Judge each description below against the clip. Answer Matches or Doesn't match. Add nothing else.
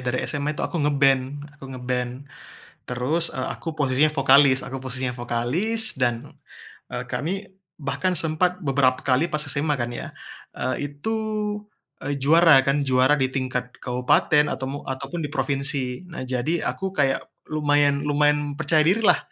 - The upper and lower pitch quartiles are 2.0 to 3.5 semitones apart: Matches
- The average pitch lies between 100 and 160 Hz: Matches